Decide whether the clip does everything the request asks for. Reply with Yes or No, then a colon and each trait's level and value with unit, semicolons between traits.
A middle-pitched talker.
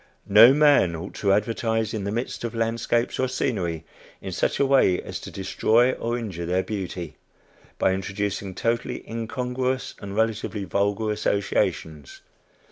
No: low, 105 Hz